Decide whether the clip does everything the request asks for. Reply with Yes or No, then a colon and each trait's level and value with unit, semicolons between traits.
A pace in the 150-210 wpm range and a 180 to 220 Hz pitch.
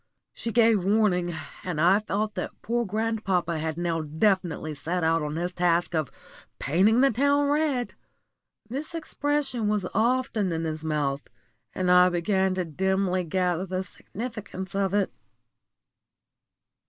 No: average, 140 wpm; high, 190 Hz